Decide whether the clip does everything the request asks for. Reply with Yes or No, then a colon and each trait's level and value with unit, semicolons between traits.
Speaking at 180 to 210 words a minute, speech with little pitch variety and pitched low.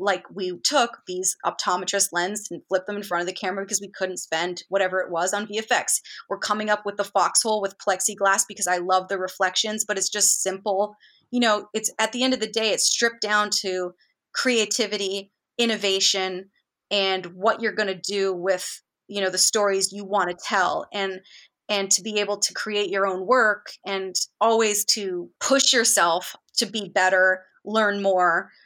No: average, 190 wpm; narrow, 2.2 semitones; high, 200 Hz